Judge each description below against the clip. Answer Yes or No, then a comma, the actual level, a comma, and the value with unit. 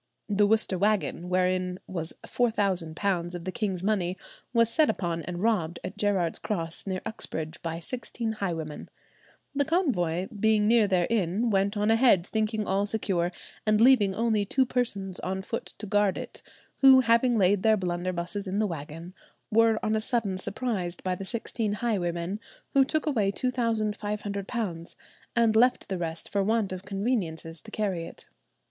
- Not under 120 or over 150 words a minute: No, average, 160 wpm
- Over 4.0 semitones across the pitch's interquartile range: No, average, 3.7 semitones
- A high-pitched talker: Yes, high, 200 Hz